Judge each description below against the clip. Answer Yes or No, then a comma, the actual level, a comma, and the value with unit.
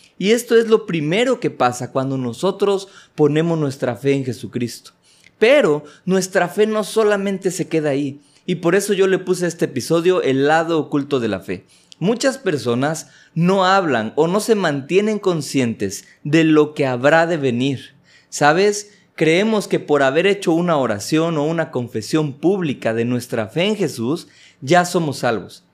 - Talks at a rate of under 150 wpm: No, average, 170 wpm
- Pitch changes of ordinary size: No, wide, 5.9 semitones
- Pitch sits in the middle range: Yes, medium, 160 Hz